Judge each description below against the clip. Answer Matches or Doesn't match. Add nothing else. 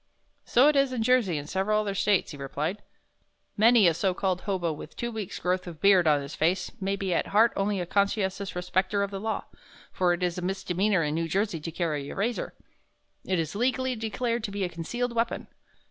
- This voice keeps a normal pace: Doesn't match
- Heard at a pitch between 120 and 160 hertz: Doesn't match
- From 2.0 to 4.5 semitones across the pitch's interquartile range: Matches